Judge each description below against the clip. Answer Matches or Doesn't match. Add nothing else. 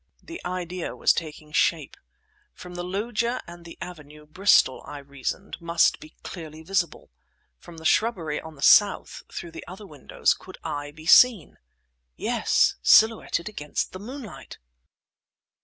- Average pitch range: Matches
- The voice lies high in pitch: Doesn't match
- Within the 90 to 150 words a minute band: Matches